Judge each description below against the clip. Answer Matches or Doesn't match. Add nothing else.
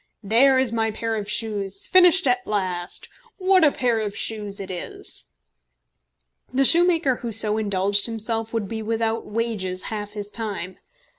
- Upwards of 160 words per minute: Doesn't match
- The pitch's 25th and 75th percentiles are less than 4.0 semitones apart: Matches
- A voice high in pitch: Matches